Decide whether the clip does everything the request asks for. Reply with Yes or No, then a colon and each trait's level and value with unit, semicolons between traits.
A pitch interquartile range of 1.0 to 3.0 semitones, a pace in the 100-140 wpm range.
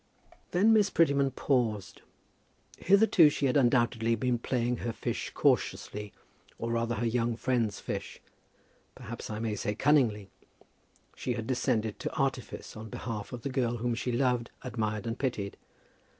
No: average, 2.7 semitones; average, 150 wpm